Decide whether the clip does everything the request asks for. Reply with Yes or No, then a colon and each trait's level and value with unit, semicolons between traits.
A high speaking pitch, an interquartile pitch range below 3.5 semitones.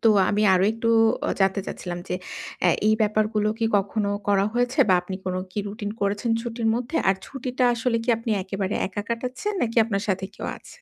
Yes: high, 215 Hz; average, 2.9 semitones